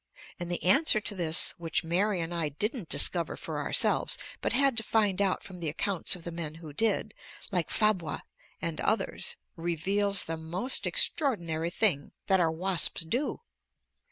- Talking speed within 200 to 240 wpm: No, average, 165 wpm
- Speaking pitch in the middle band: Yes, medium, 175 Hz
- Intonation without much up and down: No, average, 3.9 semitones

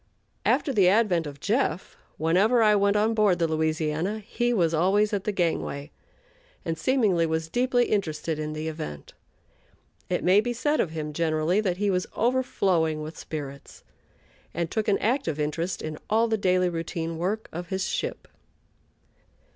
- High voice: No, medium, 180 Hz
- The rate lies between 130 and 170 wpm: Yes, average, 165 wpm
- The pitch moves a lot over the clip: No, average, 4.9 semitones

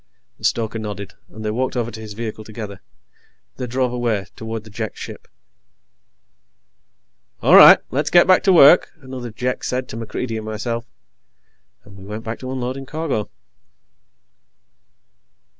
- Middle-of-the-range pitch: No, low, 115 Hz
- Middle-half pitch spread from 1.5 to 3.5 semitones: Yes, average, 2.9 semitones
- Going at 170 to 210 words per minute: No, average, 150 wpm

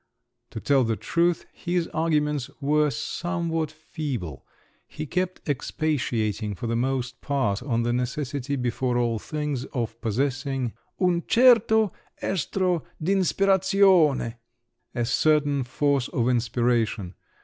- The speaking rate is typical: No, slow, 110 wpm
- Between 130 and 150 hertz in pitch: Yes, medium, 140 Hz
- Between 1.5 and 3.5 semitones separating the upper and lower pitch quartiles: No, average, 5.3 semitones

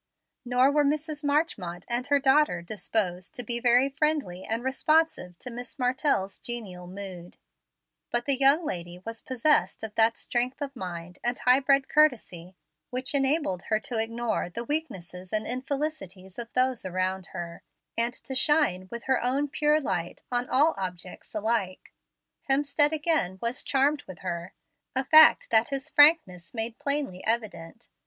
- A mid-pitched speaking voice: No, high, 240 Hz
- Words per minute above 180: No, average, 155 wpm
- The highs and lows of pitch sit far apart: Yes, wide, 7.0 semitones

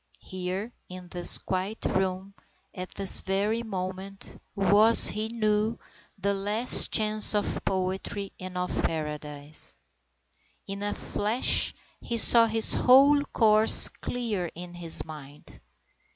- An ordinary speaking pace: No, slow, 120 wpm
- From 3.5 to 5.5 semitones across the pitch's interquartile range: No, average, 2.9 semitones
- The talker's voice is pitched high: Yes, high, 195 Hz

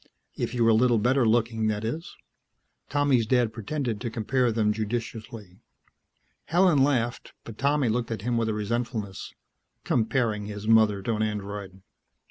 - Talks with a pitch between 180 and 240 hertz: No, low, 115 Hz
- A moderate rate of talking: Yes, average, 155 wpm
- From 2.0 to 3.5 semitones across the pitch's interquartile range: Yes, narrow, 2.5 semitones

